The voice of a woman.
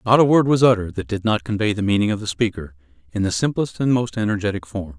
No: male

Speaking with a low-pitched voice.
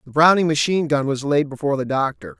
No: medium, 145 Hz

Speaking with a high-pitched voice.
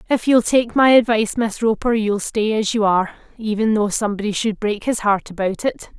Yes: high, 215 Hz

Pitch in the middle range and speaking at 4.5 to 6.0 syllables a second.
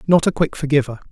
No: medium, 150 Hz; 6.7 syllables/s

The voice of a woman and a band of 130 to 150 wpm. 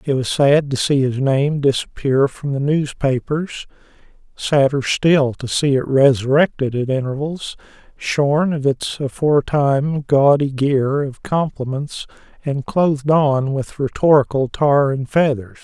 No: male; slow, 135 wpm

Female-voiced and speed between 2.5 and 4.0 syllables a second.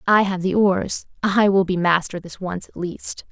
No: female; 4.3 syllables/s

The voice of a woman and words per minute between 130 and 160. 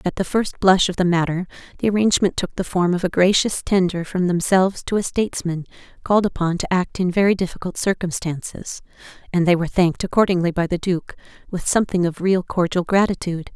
No: female; average, 185 wpm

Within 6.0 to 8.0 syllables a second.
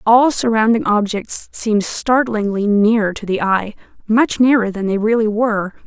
No: 4.5 syllables/s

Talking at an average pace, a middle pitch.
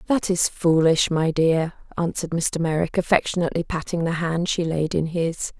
Yes: average, 170 wpm; medium, 170 Hz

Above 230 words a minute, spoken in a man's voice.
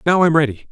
Yes: fast, 250 wpm; male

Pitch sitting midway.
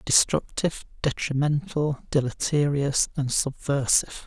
Yes: medium, 145 Hz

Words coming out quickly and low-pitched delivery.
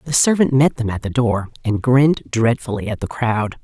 Yes: fast, 215 wpm; low, 120 Hz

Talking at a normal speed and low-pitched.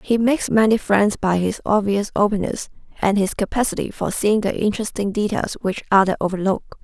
No: average, 165 wpm; high, 205 Hz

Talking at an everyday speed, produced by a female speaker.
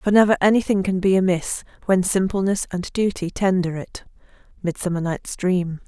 Yes: average, 165 wpm; female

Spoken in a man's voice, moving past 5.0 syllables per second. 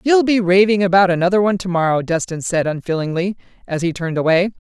No: female; 6.5 syllables/s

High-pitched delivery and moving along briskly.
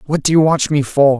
No: medium, 145 Hz; fast, 300 wpm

